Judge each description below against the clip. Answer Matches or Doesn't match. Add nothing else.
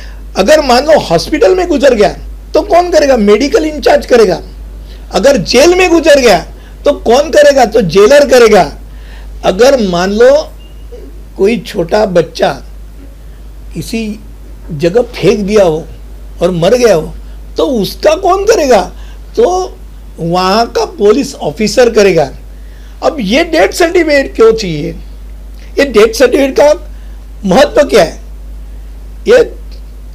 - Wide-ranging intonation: Matches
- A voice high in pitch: Matches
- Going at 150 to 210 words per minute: Doesn't match